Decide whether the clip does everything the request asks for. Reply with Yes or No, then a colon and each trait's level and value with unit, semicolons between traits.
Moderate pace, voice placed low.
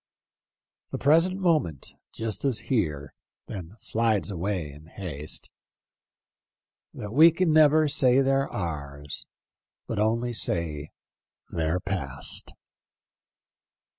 No: slow, 100 wpm; low, 105 Hz